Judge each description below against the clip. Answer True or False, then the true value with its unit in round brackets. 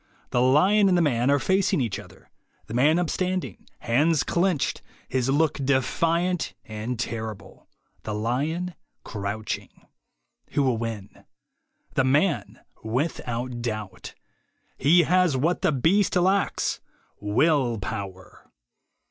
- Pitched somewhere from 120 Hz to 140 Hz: True (135 Hz)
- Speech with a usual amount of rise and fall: False (6.7 semitones)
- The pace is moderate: False (115 wpm)